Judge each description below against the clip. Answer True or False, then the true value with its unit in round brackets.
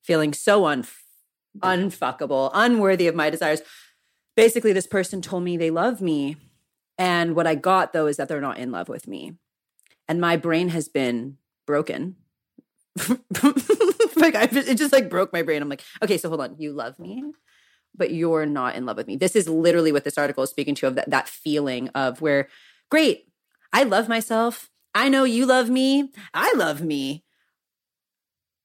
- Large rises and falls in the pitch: True (7.5 semitones)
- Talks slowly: False (180 wpm)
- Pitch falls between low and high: True (170 Hz)